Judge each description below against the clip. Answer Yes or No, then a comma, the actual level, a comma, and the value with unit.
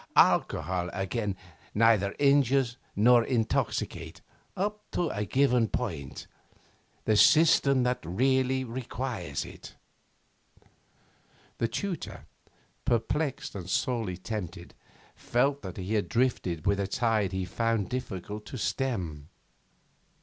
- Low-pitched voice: Yes, low, 115 Hz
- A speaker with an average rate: No, slow, 105 wpm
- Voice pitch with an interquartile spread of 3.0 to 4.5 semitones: No, average, 5.2 semitones